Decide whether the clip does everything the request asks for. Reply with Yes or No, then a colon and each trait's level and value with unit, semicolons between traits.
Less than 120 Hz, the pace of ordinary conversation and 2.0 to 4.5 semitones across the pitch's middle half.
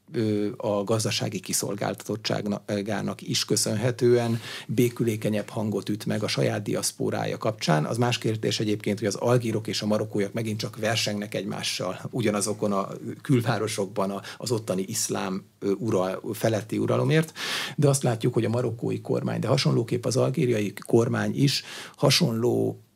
Yes: low, 110 Hz; average, 130 wpm; average, 2.8 semitones